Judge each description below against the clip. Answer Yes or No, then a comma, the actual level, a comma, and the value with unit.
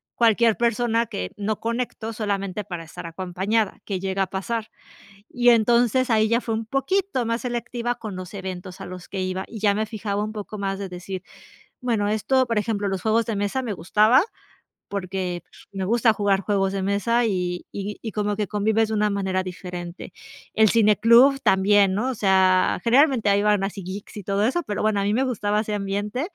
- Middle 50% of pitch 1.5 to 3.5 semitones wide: Yes, average, 3.0 semitones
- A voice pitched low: No, high, 210 Hz